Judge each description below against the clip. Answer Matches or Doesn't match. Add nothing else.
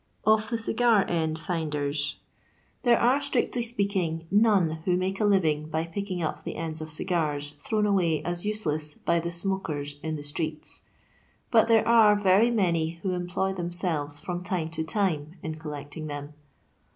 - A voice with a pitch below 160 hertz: Doesn't match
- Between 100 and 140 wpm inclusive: Doesn't match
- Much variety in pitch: Doesn't match